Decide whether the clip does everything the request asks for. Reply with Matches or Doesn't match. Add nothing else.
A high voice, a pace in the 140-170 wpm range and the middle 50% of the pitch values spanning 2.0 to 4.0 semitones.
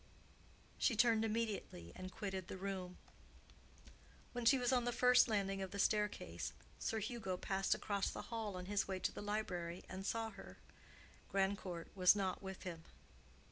Matches